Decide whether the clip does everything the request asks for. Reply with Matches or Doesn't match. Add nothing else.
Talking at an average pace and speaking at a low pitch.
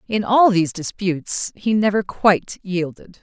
Doesn't match